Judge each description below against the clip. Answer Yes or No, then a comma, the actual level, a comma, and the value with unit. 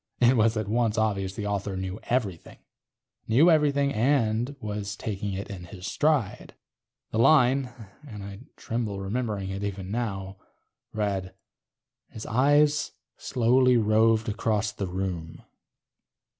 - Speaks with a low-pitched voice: Yes, low, 110 Hz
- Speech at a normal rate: No, slow, 130 wpm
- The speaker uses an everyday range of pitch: Yes, average, 3.9 semitones